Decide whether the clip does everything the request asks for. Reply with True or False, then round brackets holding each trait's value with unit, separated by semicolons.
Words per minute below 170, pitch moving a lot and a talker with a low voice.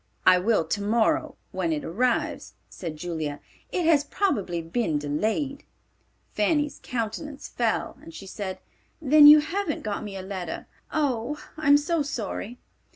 False (140 wpm; 7.9 semitones; 225 Hz)